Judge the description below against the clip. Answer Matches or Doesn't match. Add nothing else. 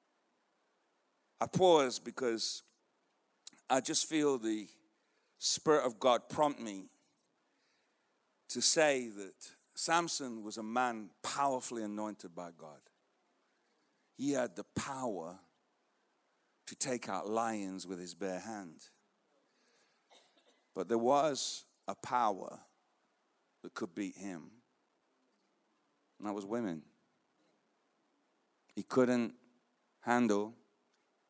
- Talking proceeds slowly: Matches